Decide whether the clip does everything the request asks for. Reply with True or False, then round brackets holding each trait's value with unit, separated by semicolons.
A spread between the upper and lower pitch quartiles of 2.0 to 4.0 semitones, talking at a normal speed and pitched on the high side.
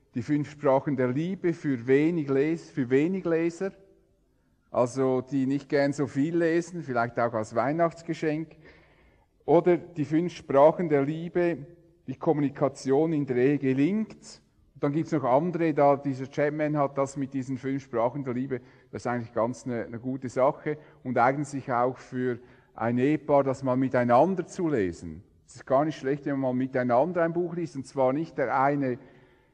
False (3.6 semitones; 170 wpm; 140 Hz)